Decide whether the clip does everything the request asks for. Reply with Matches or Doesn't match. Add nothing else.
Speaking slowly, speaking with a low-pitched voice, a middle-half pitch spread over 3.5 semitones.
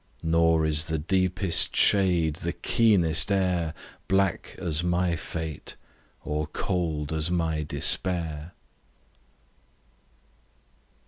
Doesn't match